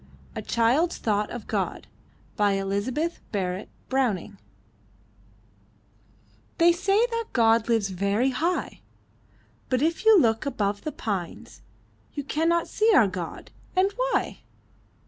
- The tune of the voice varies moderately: No, wide, 8.8 semitones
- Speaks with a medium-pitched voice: No, high, 245 Hz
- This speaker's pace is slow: Yes, slow, 115 wpm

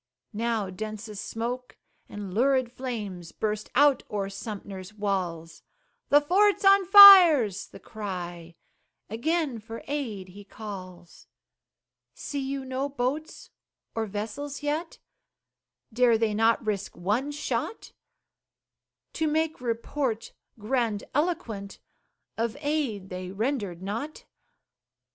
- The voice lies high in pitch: Yes, high, 225 Hz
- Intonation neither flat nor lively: No, wide, 5.9 semitones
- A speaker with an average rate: No, slow, 105 wpm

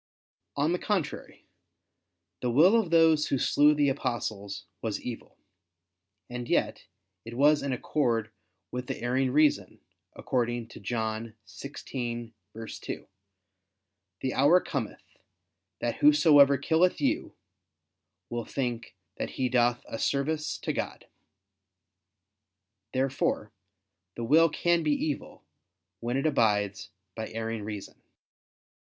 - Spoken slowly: Yes, slow, 115 wpm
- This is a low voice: Yes, low, 130 Hz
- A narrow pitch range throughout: No, average, 4.6 semitones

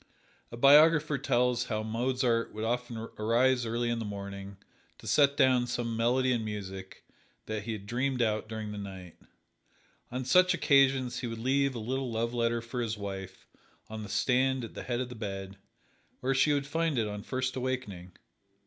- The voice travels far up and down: No, average, 3.2 semitones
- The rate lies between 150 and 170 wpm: No, average, 185 wpm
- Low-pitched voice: Yes, low, 120 Hz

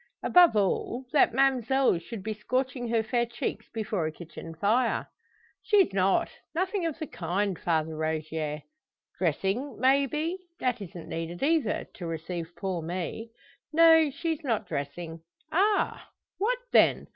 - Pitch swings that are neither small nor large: No, wide, 8.4 semitones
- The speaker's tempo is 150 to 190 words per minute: No, average, 140 wpm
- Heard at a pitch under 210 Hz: No, high, 220 Hz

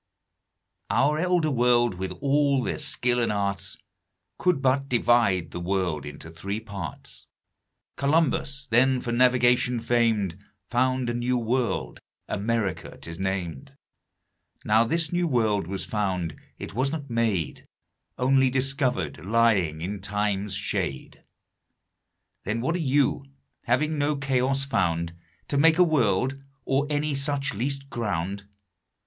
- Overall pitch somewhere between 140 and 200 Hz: No, low, 120 Hz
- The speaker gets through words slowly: Yes, slow, 130 wpm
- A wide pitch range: Yes, wide, 5.7 semitones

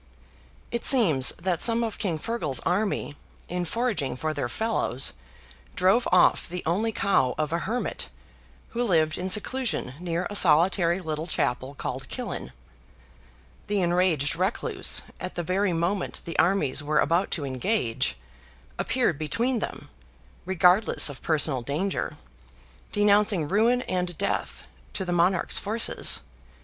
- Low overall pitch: No, medium, 180 Hz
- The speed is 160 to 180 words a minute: No, slow, 135 wpm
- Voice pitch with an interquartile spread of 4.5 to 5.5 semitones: Yes, average, 4.9 semitones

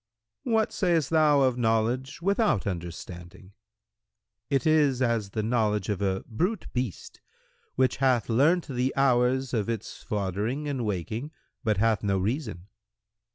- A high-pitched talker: No, low, 120 Hz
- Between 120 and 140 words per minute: Yes, slow, 135 wpm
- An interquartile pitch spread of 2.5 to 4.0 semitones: No, average, 4.8 semitones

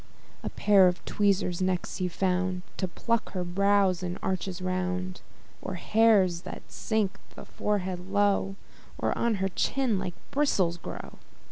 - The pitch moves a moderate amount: No, narrow, 2.0 semitones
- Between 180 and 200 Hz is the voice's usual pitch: Yes, medium, 185 Hz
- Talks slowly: No, average, 145 wpm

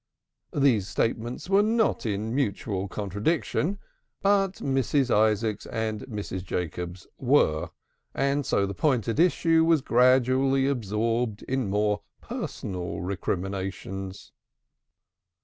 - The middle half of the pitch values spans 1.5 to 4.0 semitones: No, wide, 5.6 semitones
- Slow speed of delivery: Yes, slow, 105 wpm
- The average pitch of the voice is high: No, low, 115 Hz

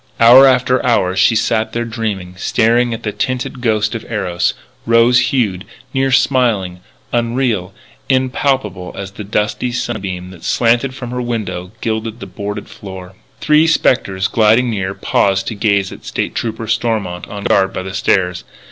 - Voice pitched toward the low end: Yes, low, 110 Hz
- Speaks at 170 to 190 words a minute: No, average, 155 wpm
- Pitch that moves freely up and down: No, average, 4.1 semitones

